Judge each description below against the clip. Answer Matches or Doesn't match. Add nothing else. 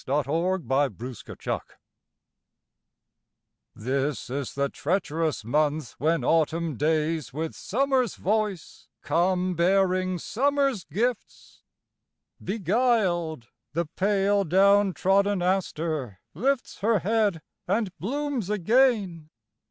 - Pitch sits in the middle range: Matches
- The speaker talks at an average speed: Doesn't match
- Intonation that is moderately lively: Matches